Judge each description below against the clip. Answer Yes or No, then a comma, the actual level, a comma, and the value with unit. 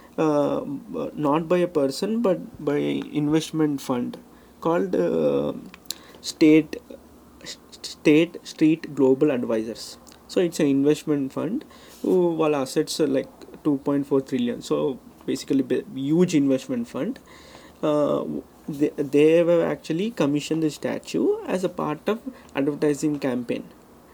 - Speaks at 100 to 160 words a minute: Yes, average, 120 wpm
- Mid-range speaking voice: Yes, medium, 150 Hz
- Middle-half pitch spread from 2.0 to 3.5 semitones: Yes, average, 3.2 semitones